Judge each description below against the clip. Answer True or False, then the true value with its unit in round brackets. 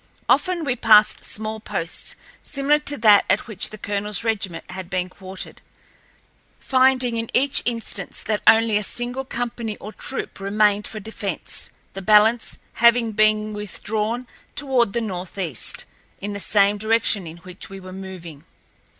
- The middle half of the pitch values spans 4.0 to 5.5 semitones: False (3.1 semitones)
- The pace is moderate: True (150 wpm)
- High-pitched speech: True (215 Hz)